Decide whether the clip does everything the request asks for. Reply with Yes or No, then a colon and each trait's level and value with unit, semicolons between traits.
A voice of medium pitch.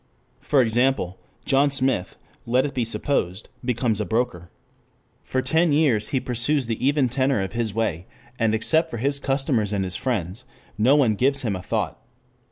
No: low, 125 Hz